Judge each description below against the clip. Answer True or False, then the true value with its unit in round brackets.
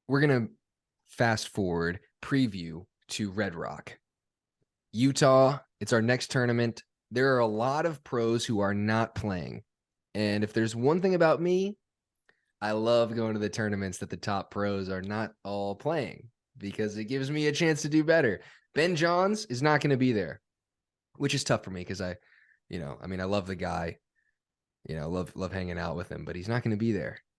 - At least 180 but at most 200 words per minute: True (195 wpm)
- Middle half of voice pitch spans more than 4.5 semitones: True (5.5 semitones)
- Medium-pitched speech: False (110 Hz)